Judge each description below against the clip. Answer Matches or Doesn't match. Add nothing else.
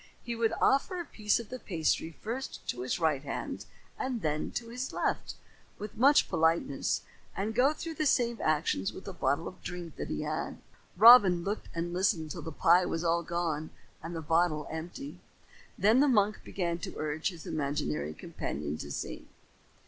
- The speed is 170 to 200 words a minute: Matches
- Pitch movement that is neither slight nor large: Doesn't match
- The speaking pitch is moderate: Matches